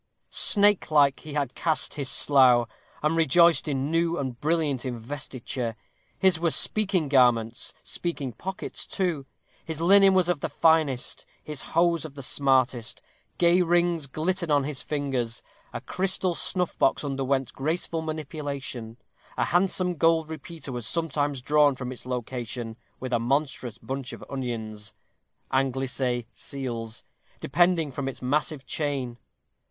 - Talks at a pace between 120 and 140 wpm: Yes, slow, 135 wpm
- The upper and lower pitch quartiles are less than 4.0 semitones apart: No, average, 4.4 semitones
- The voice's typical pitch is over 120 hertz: Yes, medium, 140 Hz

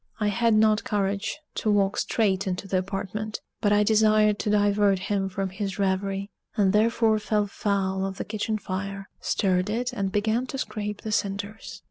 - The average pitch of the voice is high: Yes, high, 205 Hz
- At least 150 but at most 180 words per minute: Yes, average, 175 wpm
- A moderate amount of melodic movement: No, narrow, 1.7 semitones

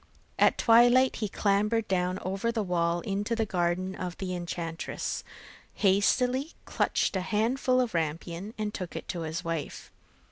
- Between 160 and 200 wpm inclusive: No, average, 150 wpm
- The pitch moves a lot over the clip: No, average, 4.6 semitones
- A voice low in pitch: No, high, 195 Hz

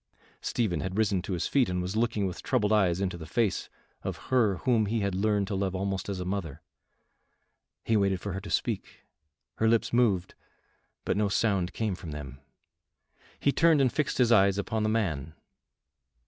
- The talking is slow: No, average, 190 wpm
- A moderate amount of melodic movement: Yes, average, 3.2 semitones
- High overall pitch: No, low, 100 Hz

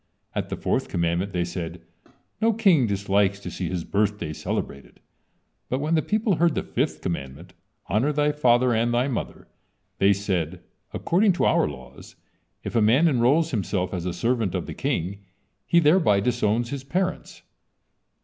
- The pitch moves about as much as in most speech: No, wide, 8.3 semitones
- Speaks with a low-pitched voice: Yes, low, 110 Hz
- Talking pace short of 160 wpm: No, average, 165 wpm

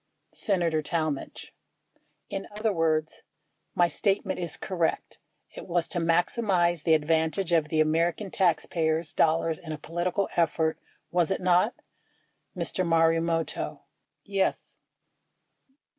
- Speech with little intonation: Yes, narrow, 2.2 semitones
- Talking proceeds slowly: Yes, slow, 115 wpm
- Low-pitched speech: No, medium, 170 Hz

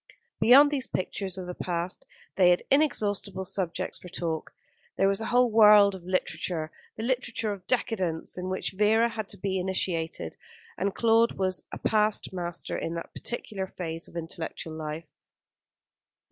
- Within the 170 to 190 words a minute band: No, average, 160 wpm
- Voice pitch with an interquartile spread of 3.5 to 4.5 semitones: Yes, average, 3.8 semitones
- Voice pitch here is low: No, high, 190 Hz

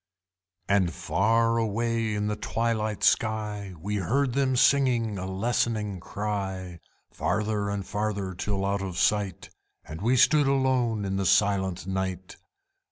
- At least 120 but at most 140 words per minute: Yes, slow, 135 wpm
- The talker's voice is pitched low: Yes, low, 105 Hz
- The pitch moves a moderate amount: Yes, average, 3.1 semitones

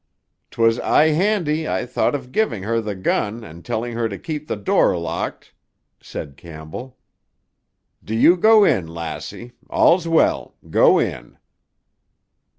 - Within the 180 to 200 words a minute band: No, average, 140 wpm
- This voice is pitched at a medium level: No, low, 115 Hz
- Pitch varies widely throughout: Yes, wide, 8.9 semitones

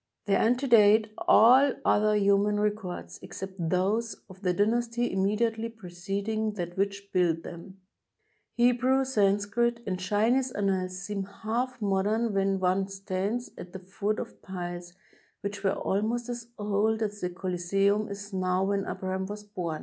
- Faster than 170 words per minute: No, average, 150 wpm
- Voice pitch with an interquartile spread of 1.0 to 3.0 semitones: Yes, narrow, 2.6 semitones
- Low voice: No, high, 200 Hz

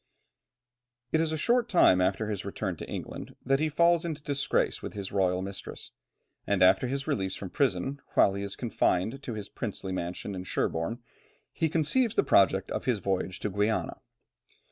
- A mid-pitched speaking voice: No, low, 105 Hz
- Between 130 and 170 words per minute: No, average, 180 wpm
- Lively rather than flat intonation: Yes, wide, 6.9 semitones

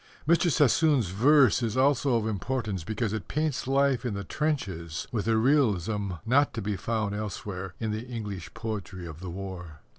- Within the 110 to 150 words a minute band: No, average, 175 wpm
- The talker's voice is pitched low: Yes, low, 110 Hz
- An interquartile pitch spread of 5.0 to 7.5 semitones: Yes, average, 5.3 semitones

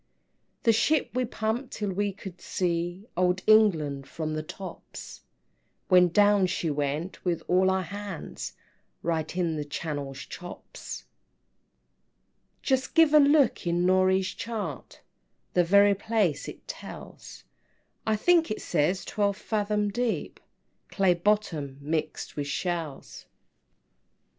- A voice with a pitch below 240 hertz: Yes, medium, 185 Hz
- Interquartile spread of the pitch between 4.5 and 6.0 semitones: No, average, 4.0 semitones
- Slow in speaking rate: Yes, slow, 125 wpm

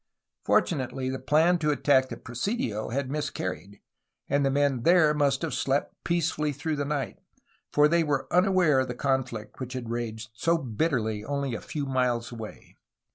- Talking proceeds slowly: No, average, 175 wpm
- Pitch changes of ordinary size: Yes, average, 3.9 semitones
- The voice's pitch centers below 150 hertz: Yes, low, 135 Hz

